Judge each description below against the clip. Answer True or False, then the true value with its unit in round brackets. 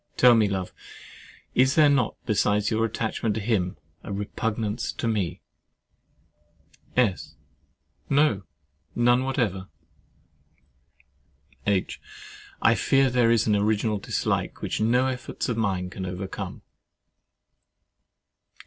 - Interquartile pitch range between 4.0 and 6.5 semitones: False (3.5 semitones)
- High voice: False (110 Hz)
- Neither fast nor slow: False (110 wpm)